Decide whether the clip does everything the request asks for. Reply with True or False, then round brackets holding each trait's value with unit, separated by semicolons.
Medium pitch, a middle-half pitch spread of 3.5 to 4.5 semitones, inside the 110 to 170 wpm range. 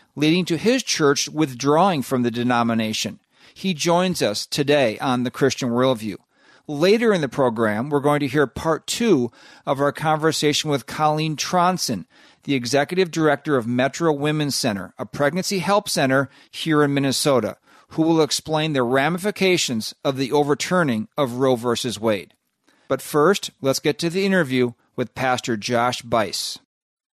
True (145 Hz; 4.1 semitones; 155 wpm)